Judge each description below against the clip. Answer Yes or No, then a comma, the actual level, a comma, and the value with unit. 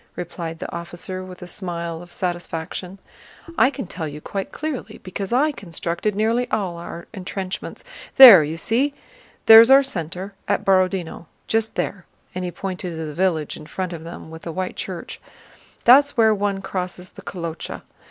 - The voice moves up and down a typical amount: Yes, average, 3.5 semitones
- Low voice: No, medium, 185 Hz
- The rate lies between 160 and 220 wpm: Yes, average, 170 wpm